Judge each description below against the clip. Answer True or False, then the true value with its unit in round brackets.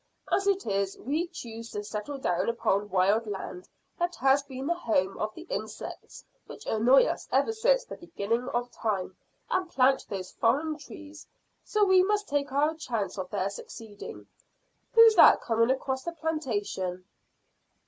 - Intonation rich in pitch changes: True (7.5 semitones)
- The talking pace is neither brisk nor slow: True (160 wpm)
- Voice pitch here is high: True (250 Hz)